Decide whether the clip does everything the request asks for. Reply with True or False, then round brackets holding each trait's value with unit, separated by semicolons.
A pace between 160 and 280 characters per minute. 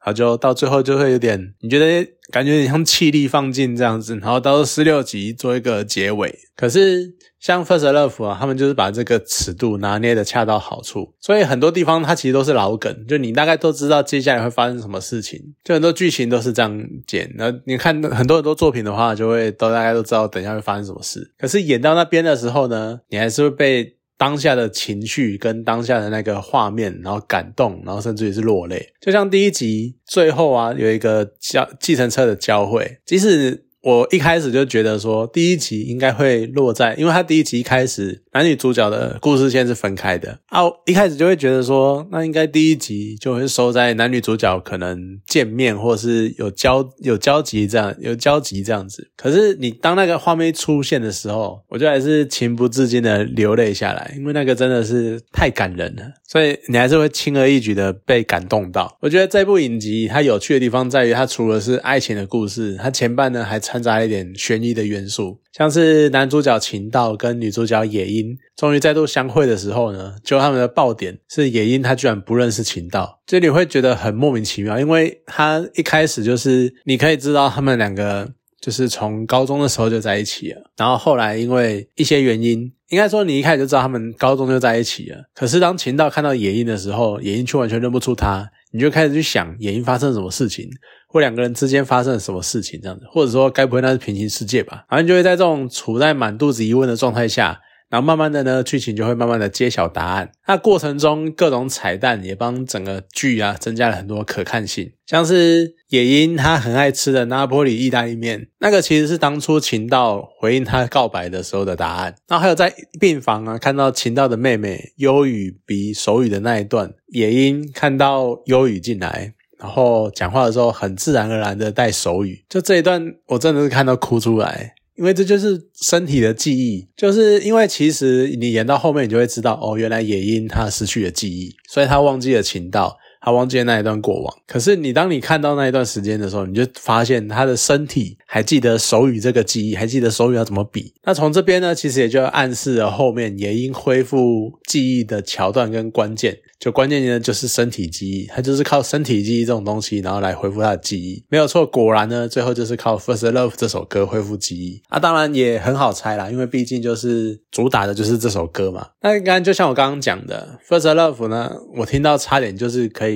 False (340 characters per minute)